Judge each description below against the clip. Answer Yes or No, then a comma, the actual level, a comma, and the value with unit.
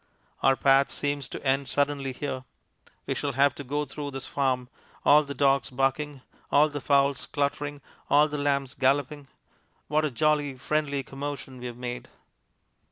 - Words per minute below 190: Yes, average, 160 wpm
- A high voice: No, medium, 140 Hz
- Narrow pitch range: Yes, narrow, 1.3 semitones